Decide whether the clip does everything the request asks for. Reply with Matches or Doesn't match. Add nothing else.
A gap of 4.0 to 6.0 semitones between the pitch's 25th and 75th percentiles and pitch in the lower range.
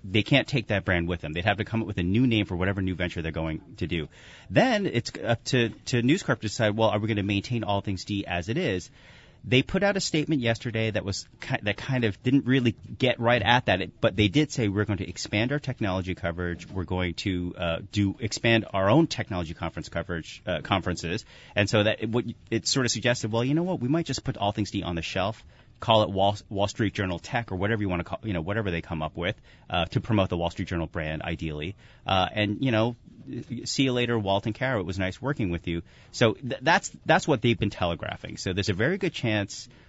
Matches